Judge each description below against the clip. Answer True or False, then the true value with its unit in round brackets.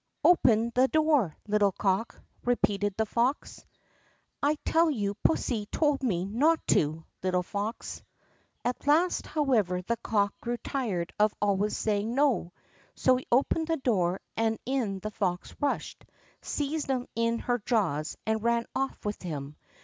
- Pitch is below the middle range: False (225 Hz)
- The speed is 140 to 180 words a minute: True (150 wpm)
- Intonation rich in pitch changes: False (5.0 semitones)